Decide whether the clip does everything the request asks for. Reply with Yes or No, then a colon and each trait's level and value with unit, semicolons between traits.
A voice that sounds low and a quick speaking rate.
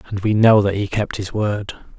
Yes: low, 100 Hz; fast, 240 wpm